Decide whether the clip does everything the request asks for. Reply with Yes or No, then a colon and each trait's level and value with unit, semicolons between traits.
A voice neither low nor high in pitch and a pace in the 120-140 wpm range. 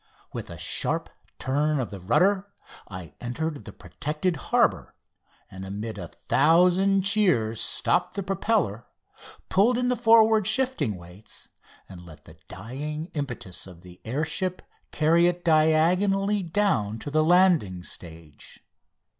Yes: medium, 155 Hz; slow, 135 wpm